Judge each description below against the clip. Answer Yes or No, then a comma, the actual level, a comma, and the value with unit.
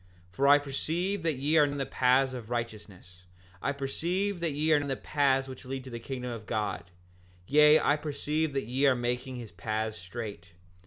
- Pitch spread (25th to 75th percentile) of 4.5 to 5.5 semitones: No, average, 3.9 semitones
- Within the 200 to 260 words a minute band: Yes, fast, 205 wpm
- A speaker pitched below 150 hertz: Yes, low, 135 Hz